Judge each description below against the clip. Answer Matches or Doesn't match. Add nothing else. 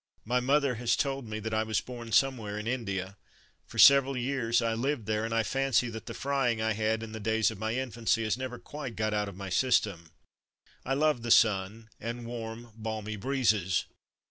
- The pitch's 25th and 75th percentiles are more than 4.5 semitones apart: Doesn't match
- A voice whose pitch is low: Matches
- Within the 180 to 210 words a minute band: Matches